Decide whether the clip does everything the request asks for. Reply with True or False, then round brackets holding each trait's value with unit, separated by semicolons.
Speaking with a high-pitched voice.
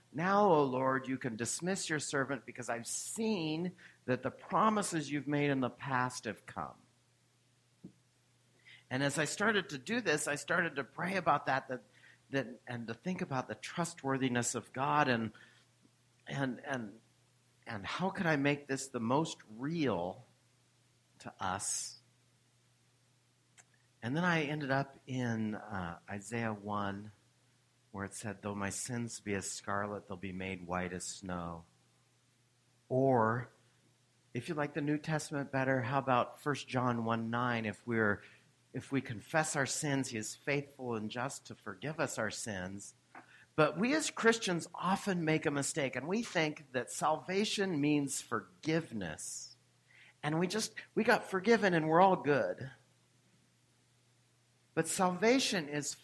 False (130 Hz)